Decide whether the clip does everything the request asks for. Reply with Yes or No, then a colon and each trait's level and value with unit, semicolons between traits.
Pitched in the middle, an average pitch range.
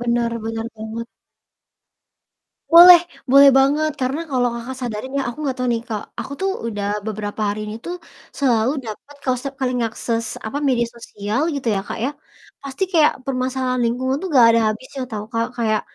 No: high, 245 Hz; average, 3.1 semitones